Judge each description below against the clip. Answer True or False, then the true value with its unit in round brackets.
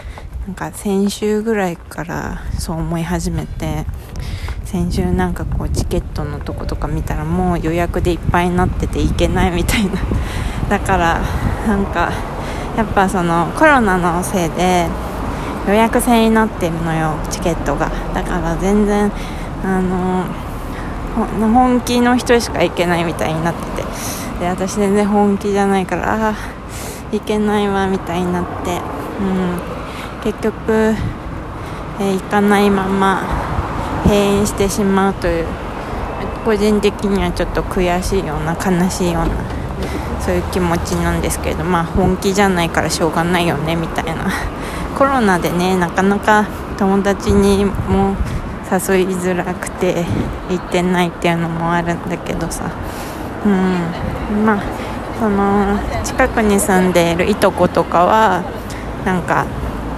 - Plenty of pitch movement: False (3.1 semitones)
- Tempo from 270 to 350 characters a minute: True (280 characters per minute)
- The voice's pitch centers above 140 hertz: True (185 Hz)